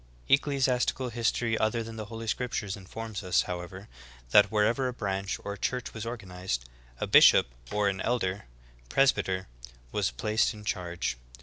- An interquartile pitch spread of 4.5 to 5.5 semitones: No, average, 3.7 semitones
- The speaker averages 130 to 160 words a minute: Yes, average, 150 wpm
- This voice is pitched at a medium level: No, low, 105 Hz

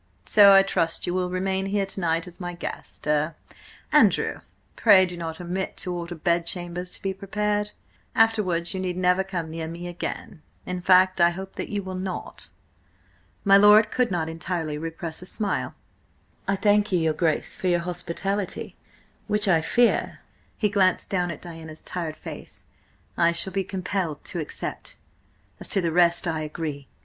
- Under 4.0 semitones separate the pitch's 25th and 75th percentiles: Yes, narrow, 2.5 semitones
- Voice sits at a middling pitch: Yes, medium, 180 Hz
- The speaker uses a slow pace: No, average, 165 wpm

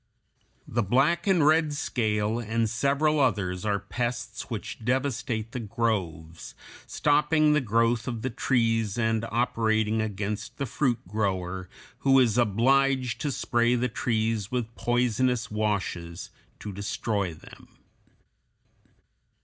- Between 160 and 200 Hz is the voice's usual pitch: No, low, 115 Hz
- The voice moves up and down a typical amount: Yes, average, 3.3 semitones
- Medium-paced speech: No, slow, 120 wpm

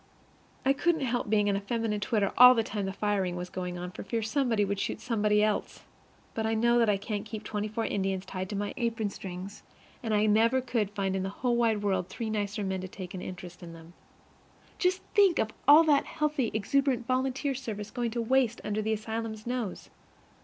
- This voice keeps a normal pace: No, fast, 215 wpm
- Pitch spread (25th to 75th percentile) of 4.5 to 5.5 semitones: No, average, 3.3 semitones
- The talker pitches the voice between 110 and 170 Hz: No, high, 215 Hz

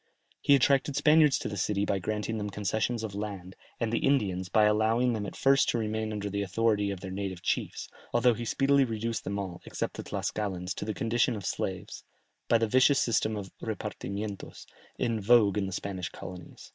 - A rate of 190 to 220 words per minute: Yes, average, 195 wpm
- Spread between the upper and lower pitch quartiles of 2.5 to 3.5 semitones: Yes, average, 2.9 semitones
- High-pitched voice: No, low, 105 Hz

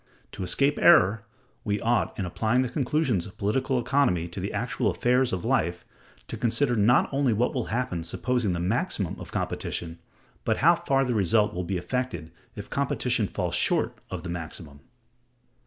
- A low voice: Yes, low, 110 Hz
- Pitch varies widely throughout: Yes, wide, 5.9 semitones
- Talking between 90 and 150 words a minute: No, average, 170 wpm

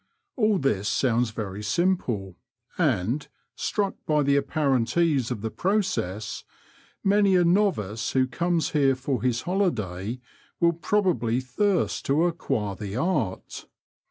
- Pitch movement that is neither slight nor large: No, wide, 7.8 semitones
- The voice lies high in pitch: No, low, 135 Hz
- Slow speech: Yes, slow, 130 wpm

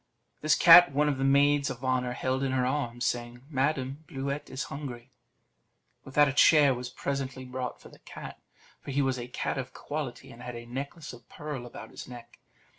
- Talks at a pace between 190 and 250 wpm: Yes, average, 200 wpm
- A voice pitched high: No, low, 130 Hz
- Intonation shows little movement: Yes, narrow, 2.3 semitones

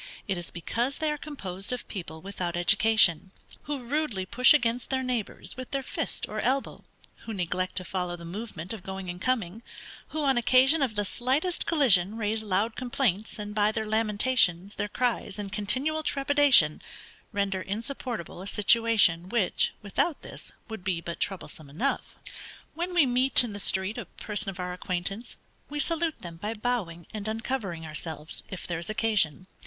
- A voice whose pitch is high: Yes, high, 215 Hz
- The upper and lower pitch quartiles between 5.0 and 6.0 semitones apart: Yes, wide, 5.5 semitones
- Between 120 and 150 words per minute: No, average, 170 wpm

